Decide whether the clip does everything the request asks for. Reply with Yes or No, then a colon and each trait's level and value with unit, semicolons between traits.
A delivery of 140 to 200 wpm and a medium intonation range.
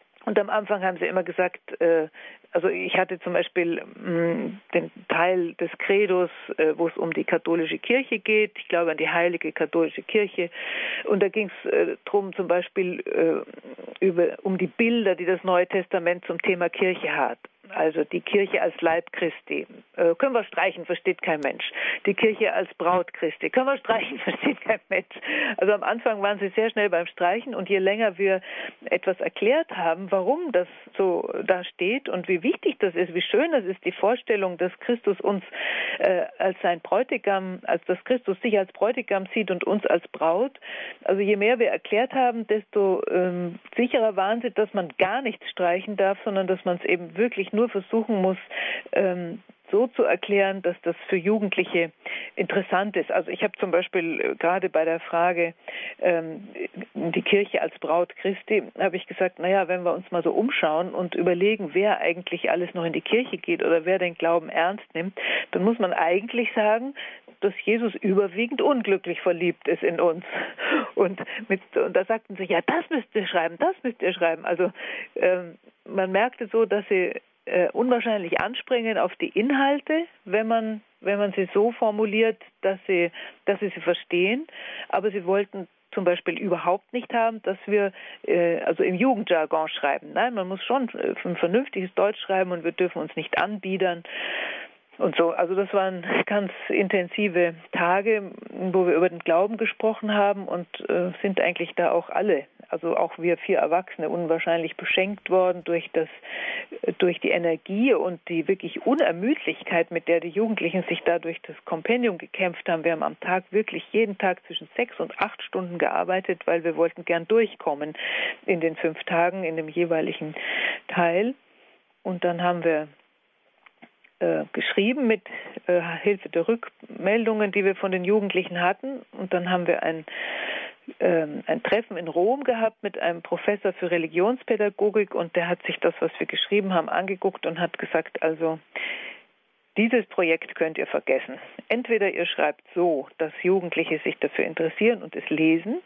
Yes: average, 170 wpm; average, 4.0 semitones